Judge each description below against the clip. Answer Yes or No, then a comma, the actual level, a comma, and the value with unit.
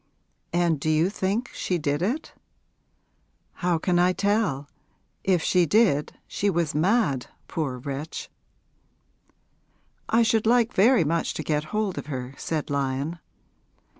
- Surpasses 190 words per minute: No, slow, 135 wpm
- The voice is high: No, medium, 170 Hz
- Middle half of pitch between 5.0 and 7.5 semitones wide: Yes, wide, 5.6 semitones